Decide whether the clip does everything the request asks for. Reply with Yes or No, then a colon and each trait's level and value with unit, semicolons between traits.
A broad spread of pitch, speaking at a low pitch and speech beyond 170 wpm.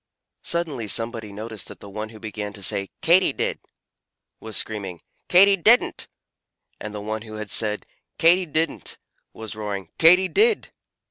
No: wide, 8.0 semitones; low, 110 Hz; average, 150 wpm